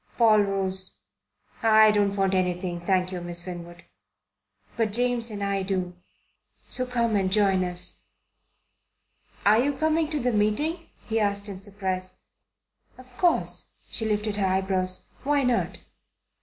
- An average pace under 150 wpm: Yes, average, 140 wpm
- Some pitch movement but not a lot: Yes, average, 3.7 semitones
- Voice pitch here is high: Yes, high, 205 Hz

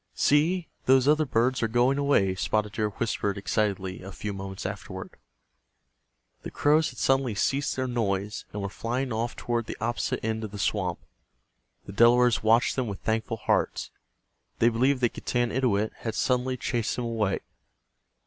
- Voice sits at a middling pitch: No, low, 115 Hz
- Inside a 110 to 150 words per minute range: No, average, 160 wpm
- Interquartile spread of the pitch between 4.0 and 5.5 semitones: No, average, 3.5 semitones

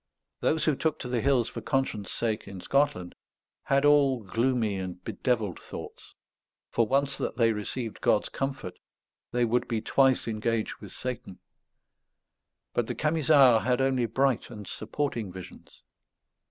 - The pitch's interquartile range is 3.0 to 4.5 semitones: Yes, average, 3.9 semitones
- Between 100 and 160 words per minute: Yes, average, 145 wpm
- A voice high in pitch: No, low, 120 Hz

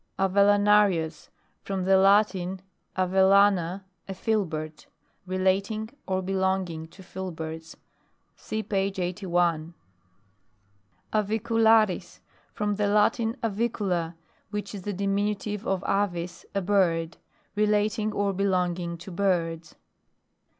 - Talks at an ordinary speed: No, slow, 100 wpm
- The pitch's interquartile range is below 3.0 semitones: Yes, narrow, 2.6 semitones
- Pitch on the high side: Yes, high, 195 Hz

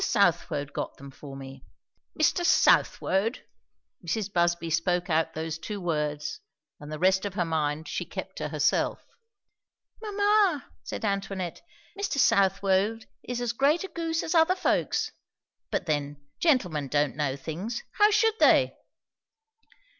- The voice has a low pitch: No, medium, 185 Hz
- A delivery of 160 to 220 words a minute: No, average, 140 wpm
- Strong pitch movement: Yes, wide, 8.3 semitones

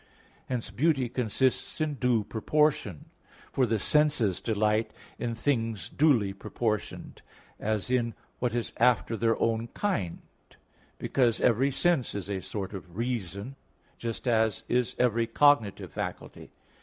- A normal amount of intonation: Yes, average, 3.1 semitones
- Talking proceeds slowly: Yes, slow, 130 wpm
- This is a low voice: Yes, low, 115 Hz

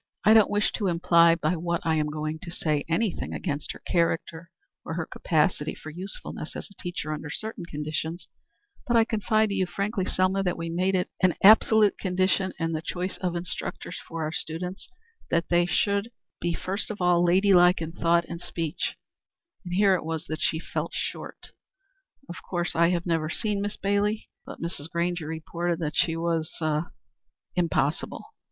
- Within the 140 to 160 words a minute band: No, average, 185 wpm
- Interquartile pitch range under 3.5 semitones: Yes, narrow, 2.5 semitones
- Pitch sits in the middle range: Yes, medium, 175 Hz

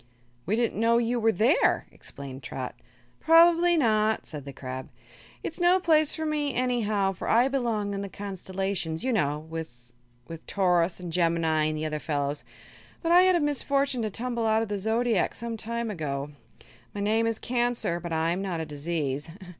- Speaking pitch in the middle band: No, high, 205 Hz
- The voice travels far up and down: Yes, wide, 7.0 semitones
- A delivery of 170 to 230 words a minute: Yes, average, 180 wpm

